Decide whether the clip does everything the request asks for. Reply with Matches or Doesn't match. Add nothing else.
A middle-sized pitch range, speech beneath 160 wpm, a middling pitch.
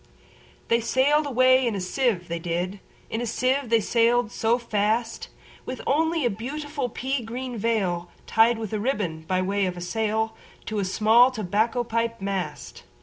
Doesn't match